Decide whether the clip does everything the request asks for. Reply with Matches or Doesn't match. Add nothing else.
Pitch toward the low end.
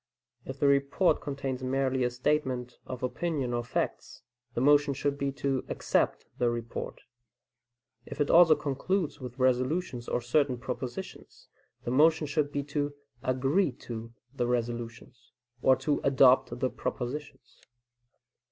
Matches